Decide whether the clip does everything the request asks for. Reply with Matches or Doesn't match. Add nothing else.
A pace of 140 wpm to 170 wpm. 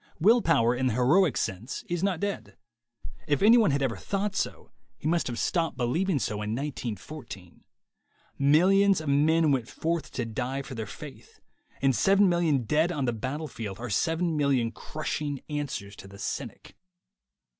Matches